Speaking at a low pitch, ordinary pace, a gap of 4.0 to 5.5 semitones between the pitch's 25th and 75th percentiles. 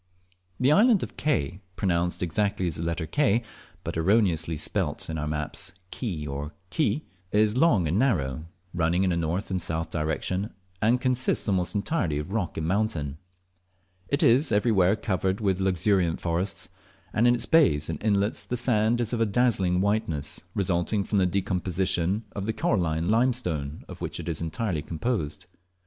Yes: very low, 95 Hz; average, 165 wpm; average, 5.1 semitones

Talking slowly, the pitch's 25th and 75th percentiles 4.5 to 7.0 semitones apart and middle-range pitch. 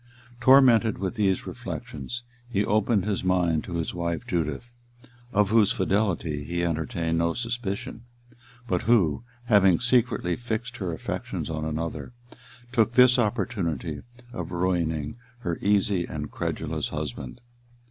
No: slow, 125 wpm; wide, 5.4 semitones; very low, 95 Hz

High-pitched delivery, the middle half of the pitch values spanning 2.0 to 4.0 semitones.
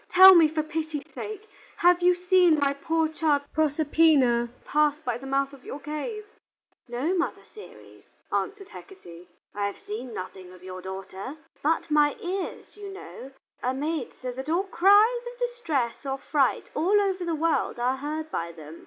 No: very high, 305 Hz; wide, 5.6 semitones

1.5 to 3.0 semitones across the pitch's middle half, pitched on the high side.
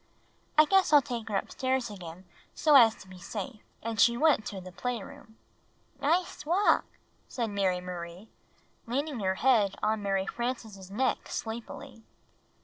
No: average, 5.1 semitones; high, 225 Hz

